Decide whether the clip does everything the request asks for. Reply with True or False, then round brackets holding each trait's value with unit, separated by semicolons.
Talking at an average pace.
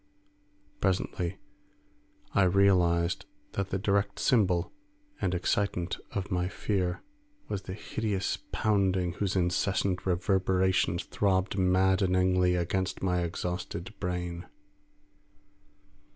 False (95 wpm)